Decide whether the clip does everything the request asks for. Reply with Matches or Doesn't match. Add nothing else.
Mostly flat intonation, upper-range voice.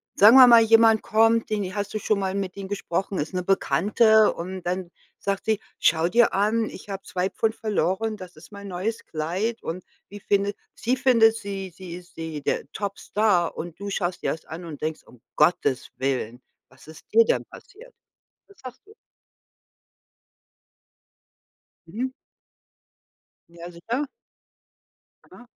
Doesn't match